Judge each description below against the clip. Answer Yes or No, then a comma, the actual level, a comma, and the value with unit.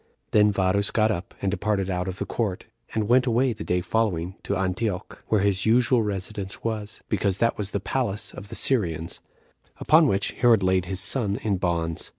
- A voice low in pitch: Yes, low, 100 Hz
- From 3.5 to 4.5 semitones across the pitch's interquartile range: No, average, 3.1 semitones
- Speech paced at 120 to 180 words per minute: No, average, 190 wpm